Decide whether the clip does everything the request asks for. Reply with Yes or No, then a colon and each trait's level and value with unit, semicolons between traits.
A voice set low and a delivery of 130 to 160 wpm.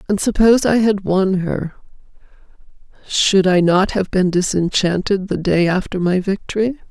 No: high, 190 Hz; average, 150 wpm